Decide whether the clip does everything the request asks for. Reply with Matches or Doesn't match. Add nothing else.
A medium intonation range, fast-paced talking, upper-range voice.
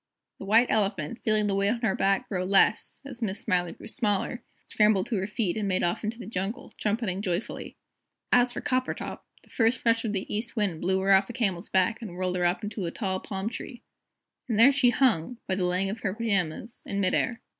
Matches